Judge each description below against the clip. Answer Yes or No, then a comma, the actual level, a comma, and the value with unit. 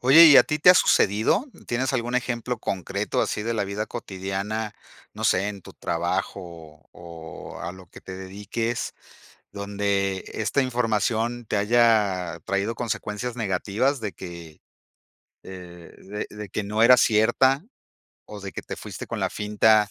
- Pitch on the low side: Yes, low, 105 Hz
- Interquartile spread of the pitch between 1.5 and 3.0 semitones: No, average, 3.6 semitones